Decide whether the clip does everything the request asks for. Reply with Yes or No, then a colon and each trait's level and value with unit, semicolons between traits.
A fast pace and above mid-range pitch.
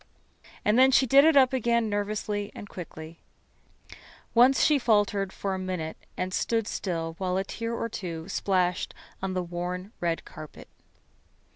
No: average, 155 wpm; high, 195 Hz